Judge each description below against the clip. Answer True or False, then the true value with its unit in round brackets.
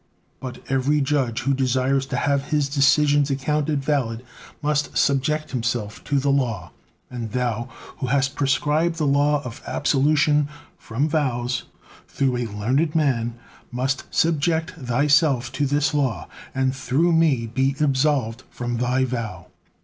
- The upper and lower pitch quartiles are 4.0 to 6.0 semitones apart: False (3.0 semitones)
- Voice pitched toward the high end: False (135 Hz)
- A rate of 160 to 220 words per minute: False (140 wpm)